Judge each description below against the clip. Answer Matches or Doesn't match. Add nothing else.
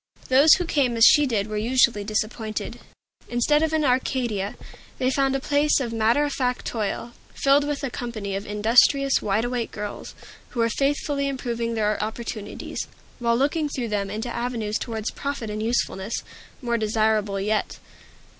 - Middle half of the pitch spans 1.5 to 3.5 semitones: Doesn't match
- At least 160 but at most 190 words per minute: Matches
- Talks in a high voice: Matches